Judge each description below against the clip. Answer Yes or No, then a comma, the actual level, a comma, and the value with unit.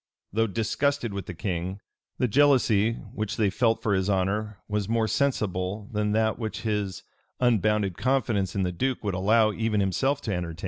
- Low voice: Yes, low, 105 Hz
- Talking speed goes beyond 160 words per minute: Yes, average, 180 wpm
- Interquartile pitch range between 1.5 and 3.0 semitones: Yes, average, 2.7 semitones